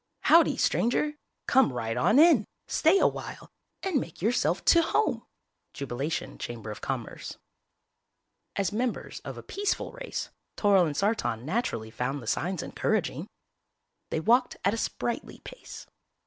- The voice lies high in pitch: Yes, high, 205 Hz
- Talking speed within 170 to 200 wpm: No, slow, 135 wpm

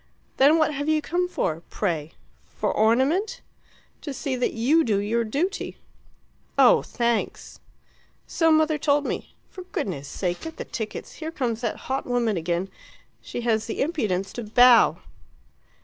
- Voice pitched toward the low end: No, high, 245 Hz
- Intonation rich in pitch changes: Yes, wide, 6.3 semitones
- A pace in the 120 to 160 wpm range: Yes, average, 150 wpm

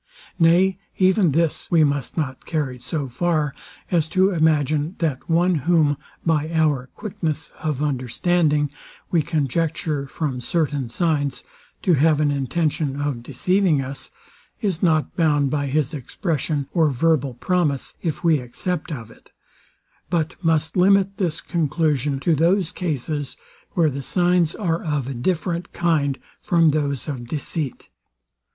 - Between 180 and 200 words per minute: No, average, 140 wpm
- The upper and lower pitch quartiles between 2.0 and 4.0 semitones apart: Yes, average, 3.3 semitones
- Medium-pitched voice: Yes, medium, 155 Hz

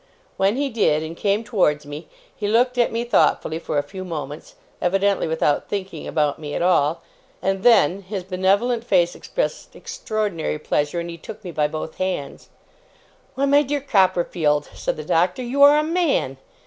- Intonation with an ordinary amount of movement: No, wide, 6.3 semitones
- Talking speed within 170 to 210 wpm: Yes, average, 175 wpm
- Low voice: No, medium, 185 Hz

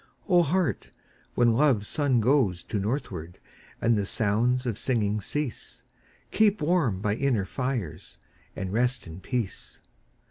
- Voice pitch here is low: Yes, low, 120 Hz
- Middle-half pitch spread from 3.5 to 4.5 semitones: No, average, 5.2 semitones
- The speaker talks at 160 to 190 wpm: No, slow, 135 wpm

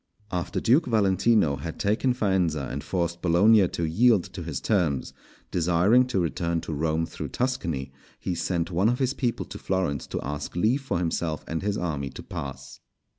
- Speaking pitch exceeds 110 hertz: No, very low, 90 Hz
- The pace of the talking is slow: No, average, 175 wpm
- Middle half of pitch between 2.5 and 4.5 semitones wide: No, average, 4.9 semitones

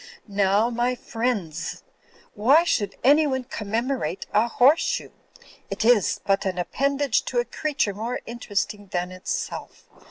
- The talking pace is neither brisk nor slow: No, slow, 130 wpm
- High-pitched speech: Yes, high, 235 Hz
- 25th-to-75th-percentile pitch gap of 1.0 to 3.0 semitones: No, average, 4.7 semitones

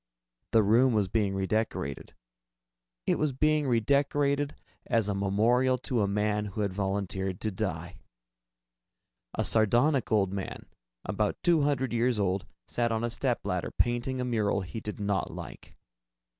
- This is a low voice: Yes, low, 110 Hz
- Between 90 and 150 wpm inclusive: Yes, average, 145 wpm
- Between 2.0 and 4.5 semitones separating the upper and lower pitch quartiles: Yes, average, 4.2 semitones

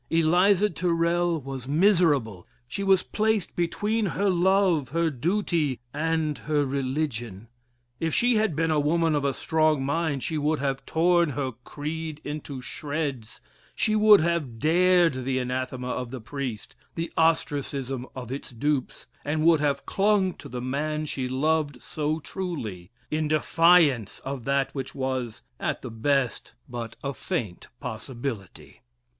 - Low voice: No, medium, 150 Hz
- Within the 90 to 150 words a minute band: Yes, average, 145 wpm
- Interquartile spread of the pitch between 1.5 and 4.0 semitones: No, average, 4.4 semitones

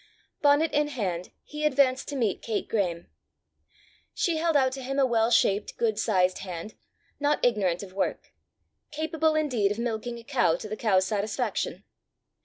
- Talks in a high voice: Yes, high, 235 Hz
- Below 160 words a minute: No, average, 165 wpm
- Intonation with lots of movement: Yes, wide, 6.2 semitones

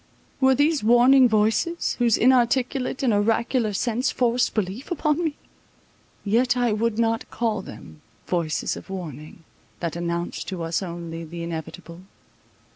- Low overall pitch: No, high, 220 Hz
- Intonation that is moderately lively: No, wide, 6.4 semitones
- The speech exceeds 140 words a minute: No, slow, 135 wpm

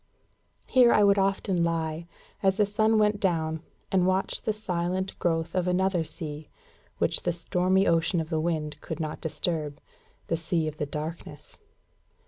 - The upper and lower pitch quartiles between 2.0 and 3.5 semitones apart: Yes, average, 3.1 semitones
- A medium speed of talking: Yes, average, 160 wpm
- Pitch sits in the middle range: Yes, medium, 175 Hz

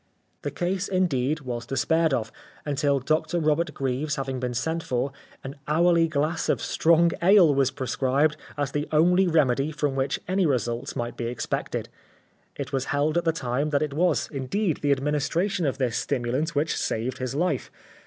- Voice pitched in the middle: Yes, medium, 145 Hz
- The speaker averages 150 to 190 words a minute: Yes, average, 175 wpm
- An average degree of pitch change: Yes, average, 3.8 semitones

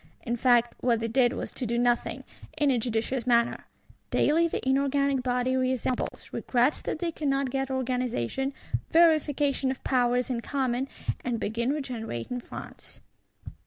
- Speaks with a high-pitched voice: Yes, very high, 255 Hz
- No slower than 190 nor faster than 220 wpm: No, average, 145 wpm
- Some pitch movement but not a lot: No, narrow, 2.2 semitones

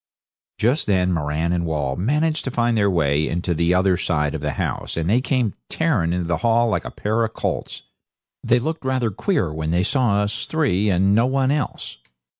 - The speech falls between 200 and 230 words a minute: Yes, fast, 205 wpm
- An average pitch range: No, wide, 6.5 semitones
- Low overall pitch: Yes, low, 100 Hz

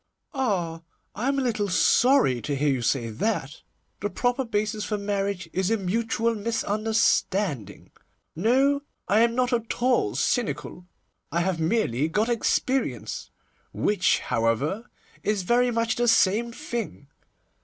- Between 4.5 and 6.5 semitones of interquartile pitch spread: Yes, average, 5.1 semitones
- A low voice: No, high, 210 Hz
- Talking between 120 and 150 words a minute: Yes, slow, 135 wpm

